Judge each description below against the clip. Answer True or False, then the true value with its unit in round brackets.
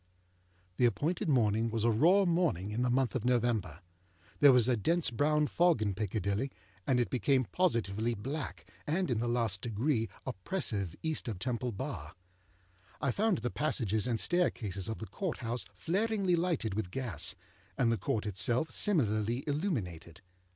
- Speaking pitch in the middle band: False (120 Hz)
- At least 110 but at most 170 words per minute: True (160 wpm)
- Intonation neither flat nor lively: False (6.1 semitones)